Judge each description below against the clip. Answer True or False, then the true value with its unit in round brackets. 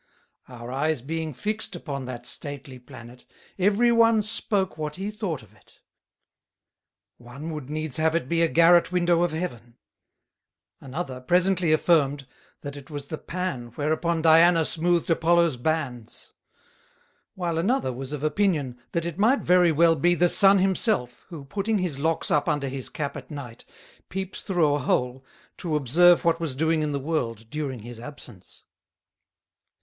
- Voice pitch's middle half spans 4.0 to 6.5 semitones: True (4.5 semitones)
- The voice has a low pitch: False (155 Hz)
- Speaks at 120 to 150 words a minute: False (160 wpm)